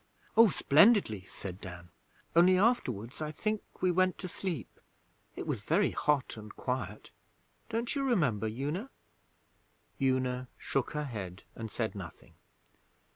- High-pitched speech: No, low, 135 Hz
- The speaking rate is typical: No, slow, 130 wpm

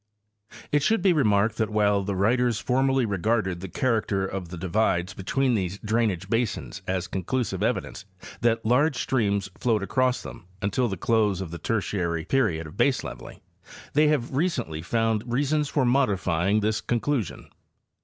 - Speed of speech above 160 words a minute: No, average, 155 wpm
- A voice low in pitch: Yes, low, 110 Hz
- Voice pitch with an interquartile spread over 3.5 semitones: Yes, average, 4.6 semitones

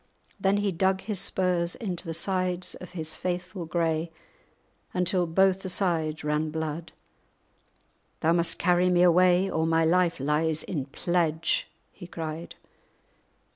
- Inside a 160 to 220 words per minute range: No, slow, 135 wpm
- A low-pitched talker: No, medium, 175 Hz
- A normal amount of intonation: No, narrow, 2.2 semitones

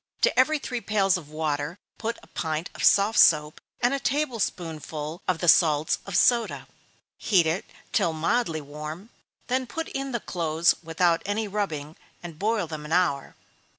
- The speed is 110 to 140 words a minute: No, average, 170 wpm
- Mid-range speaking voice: Yes, medium, 175 Hz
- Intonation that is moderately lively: No, wide, 6.0 semitones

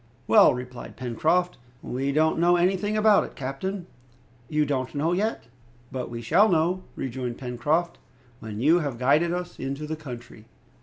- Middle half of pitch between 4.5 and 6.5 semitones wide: Yes, wide, 5.6 semitones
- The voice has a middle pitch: Yes, medium, 150 Hz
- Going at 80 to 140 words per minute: No, average, 155 wpm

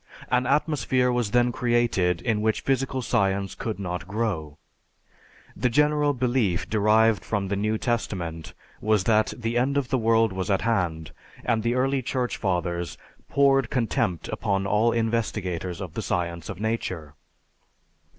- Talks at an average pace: Yes, average, 150 wpm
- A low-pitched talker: Yes, low, 110 Hz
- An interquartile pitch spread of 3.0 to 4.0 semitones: No, average, 4.4 semitones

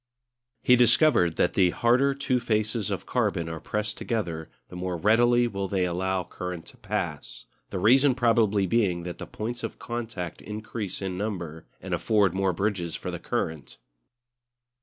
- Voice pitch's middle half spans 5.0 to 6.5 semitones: No, average, 4.6 semitones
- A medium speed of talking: Yes, average, 160 wpm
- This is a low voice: Yes, low, 100 Hz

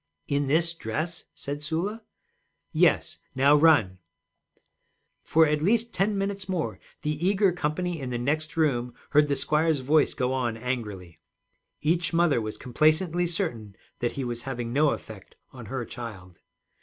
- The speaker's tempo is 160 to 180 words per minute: No, average, 150 wpm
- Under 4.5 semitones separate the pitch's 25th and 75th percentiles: No, wide, 5.5 semitones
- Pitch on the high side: No, medium, 150 Hz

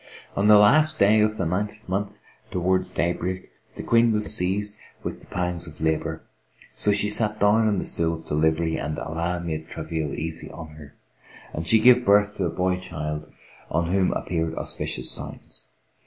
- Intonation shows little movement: No, average, 4.2 semitones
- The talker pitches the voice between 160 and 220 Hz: No, very low, 90 Hz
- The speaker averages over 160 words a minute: Yes, average, 185 wpm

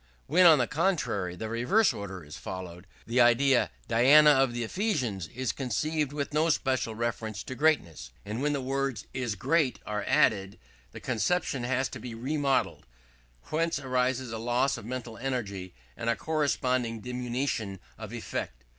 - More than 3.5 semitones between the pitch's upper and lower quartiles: Yes, average, 4.3 semitones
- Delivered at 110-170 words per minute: Yes, average, 160 wpm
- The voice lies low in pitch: Yes, low, 125 Hz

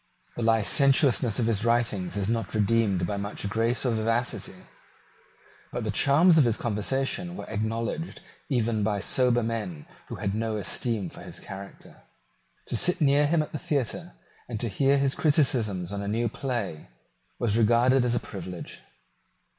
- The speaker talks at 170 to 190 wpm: No, average, 160 wpm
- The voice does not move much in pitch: No, average, 4.1 semitones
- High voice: No, low, 115 Hz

